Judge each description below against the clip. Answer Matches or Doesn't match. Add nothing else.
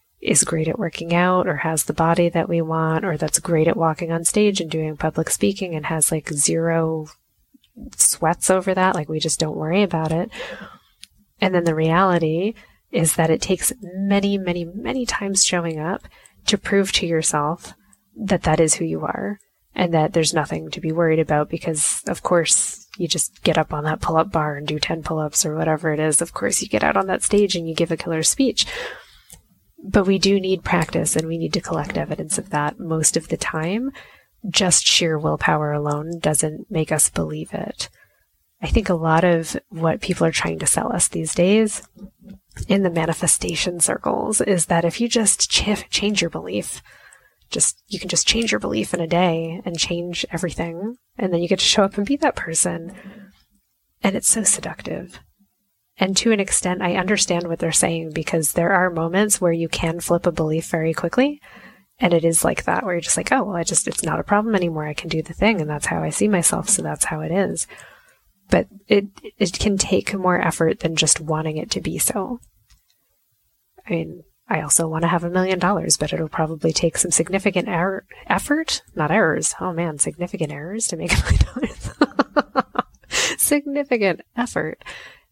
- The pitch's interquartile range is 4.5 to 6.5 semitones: Doesn't match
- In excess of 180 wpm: Matches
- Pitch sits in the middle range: Matches